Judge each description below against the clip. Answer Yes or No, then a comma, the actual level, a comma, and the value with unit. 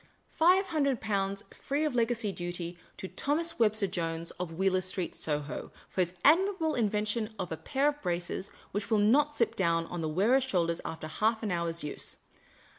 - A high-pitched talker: Yes, high, 200 Hz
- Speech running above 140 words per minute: Yes, average, 185 wpm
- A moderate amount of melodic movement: No, wide, 7.2 semitones